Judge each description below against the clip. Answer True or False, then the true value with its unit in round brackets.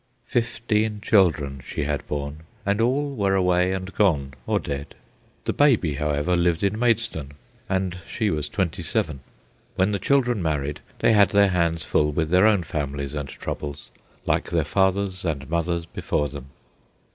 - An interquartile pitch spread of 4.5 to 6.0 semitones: True (5.4 semitones)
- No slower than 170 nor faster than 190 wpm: False (160 wpm)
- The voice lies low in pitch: True (90 Hz)